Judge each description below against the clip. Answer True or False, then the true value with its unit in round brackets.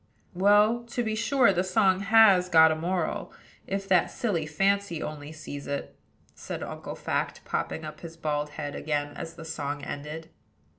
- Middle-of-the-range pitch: True (170 Hz)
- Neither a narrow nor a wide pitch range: True (4.7 semitones)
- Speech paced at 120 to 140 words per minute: False (165 wpm)